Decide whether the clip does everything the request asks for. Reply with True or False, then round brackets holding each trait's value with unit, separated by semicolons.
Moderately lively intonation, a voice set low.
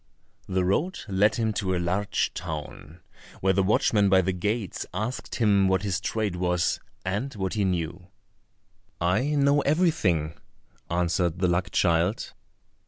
True (3.3 semitones; 95 Hz)